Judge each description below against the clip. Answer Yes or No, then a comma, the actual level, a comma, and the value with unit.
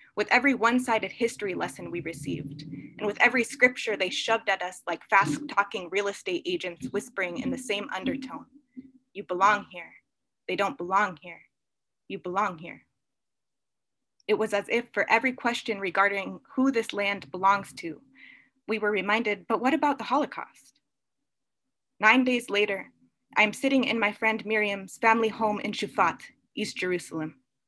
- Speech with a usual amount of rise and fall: Yes, average, 3.9 semitones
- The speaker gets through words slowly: No, average, 160 wpm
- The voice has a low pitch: No, high, 210 Hz